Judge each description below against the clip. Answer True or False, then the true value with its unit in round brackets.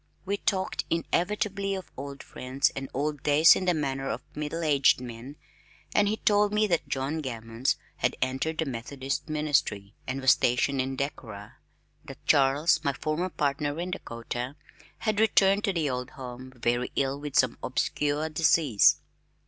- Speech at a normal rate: True (160 wpm)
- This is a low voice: False (145 Hz)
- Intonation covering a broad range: False (4.3 semitones)